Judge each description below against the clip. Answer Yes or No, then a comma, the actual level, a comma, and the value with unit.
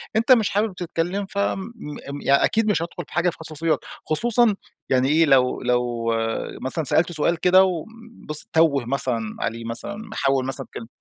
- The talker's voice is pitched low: No, medium, 160 Hz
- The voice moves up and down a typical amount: No, wide, 6.5 semitones